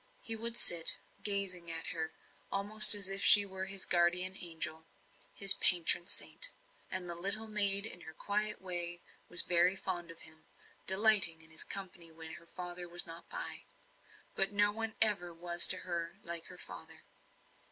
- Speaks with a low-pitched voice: No, medium, 180 Hz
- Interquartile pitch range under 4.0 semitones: Yes, average, 2.8 semitones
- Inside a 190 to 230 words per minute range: No, average, 170 wpm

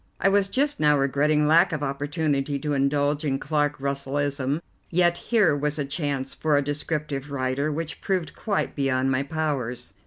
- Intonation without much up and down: Yes, narrow, 2.2 semitones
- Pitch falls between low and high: Yes, medium, 145 Hz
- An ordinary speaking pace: Yes, average, 165 wpm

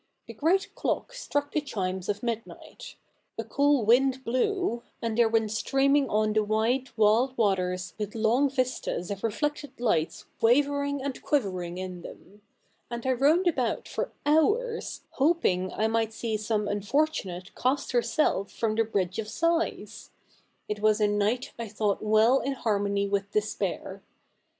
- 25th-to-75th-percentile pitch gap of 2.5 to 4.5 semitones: No, average, 5.0 semitones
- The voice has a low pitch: No, high, 225 Hz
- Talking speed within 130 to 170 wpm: Yes, average, 150 wpm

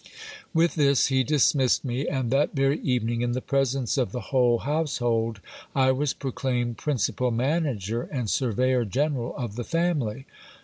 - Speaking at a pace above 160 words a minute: No, average, 150 wpm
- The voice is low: Yes, low, 130 Hz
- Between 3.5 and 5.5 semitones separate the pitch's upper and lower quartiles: No, average, 2.7 semitones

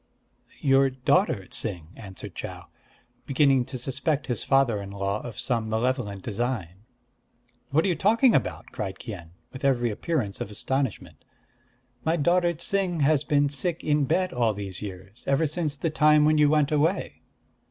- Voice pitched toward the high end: No, low, 135 Hz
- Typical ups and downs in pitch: No, wide, 6.2 semitones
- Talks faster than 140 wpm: Yes, average, 160 wpm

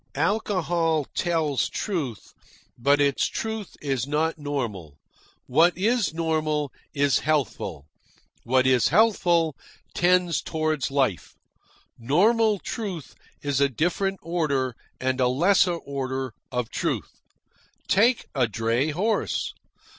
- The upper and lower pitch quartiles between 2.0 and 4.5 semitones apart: No, average, 5.1 semitones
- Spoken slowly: Yes, slow, 110 wpm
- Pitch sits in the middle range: Yes, medium, 150 Hz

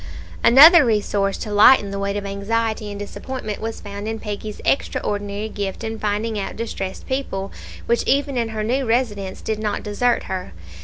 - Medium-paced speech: Yes, average, 170 wpm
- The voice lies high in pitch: Yes, high, 215 Hz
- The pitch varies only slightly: Yes, narrow, 2.3 semitones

